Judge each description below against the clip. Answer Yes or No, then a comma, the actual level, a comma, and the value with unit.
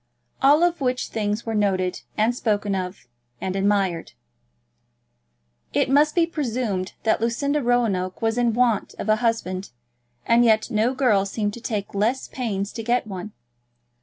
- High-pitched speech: Yes, high, 220 Hz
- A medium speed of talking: Yes, average, 155 wpm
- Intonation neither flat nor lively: Yes, average, 3.5 semitones